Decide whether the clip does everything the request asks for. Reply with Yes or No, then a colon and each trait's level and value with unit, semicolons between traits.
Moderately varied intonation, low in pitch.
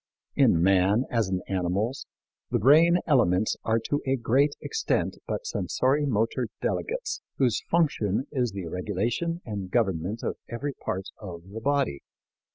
No: wide, 6.8 semitones; low, 115 Hz